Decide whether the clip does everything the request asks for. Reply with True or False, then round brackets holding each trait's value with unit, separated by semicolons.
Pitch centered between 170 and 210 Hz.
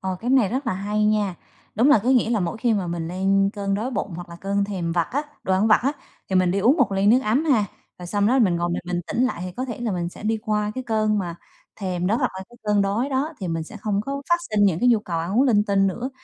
True (205 Hz)